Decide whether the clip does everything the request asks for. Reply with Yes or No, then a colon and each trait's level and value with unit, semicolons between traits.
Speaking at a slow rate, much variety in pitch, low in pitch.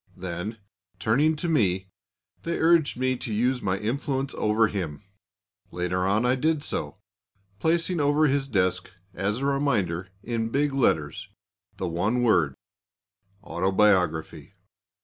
Yes: slow, 130 wpm; wide, 6.9 semitones; low, 110 Hz